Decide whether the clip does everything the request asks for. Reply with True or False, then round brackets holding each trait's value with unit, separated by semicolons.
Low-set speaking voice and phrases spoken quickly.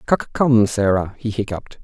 False (105 Hz; 165 wpm)